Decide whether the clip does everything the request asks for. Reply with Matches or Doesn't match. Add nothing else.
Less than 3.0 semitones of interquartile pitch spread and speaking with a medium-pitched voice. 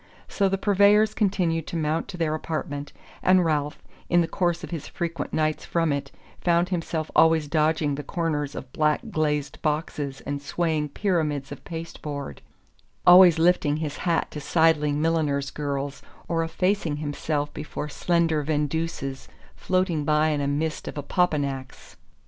Matches